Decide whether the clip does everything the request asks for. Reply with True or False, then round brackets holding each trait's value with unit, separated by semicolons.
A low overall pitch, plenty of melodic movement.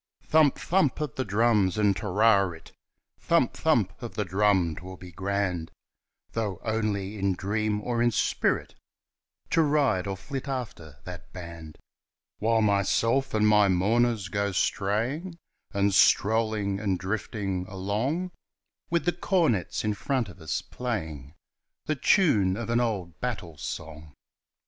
False (105 Hz; 4.1 semitones)